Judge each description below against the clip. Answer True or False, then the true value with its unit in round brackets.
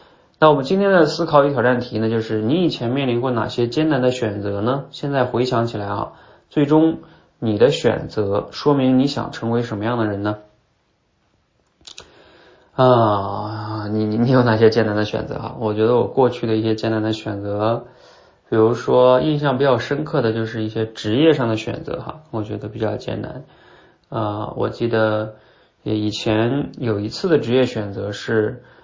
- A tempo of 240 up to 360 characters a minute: True (260 characters per minute)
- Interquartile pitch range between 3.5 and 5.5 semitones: False (3.1 semitones)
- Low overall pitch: True (115 Hz)